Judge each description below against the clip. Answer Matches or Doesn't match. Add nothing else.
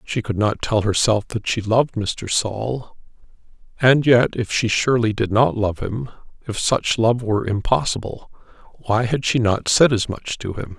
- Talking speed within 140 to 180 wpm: Matches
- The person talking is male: Matches